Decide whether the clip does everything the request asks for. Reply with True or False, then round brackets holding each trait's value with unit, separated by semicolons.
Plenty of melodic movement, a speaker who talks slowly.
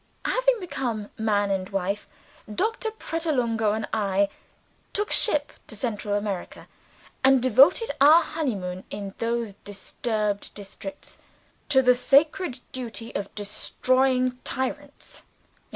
True (5.7 semitones; 115 wpm)